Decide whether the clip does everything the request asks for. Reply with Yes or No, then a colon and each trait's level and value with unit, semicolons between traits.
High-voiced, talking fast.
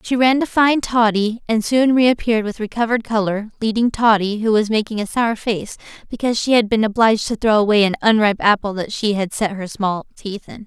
Yes: high, 220 Hz; fast, 215 wpm